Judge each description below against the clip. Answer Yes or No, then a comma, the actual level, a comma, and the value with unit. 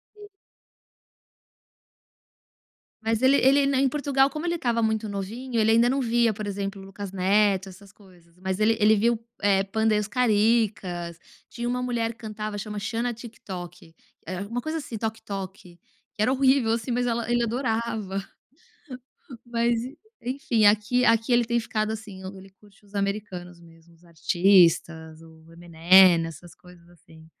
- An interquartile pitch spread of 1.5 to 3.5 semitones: No, average, 4.0 semitones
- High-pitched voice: Yes, high, 215 Hz